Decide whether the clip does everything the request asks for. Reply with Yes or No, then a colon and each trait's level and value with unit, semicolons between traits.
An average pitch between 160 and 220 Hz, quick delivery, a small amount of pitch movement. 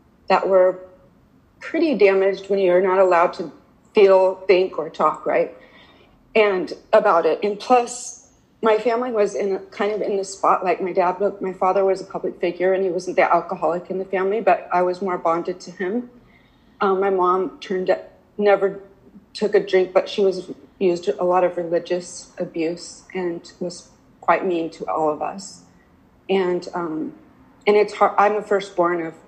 No: high, 190 Hz; average, 180 wpm; narrow, 2.1 semitones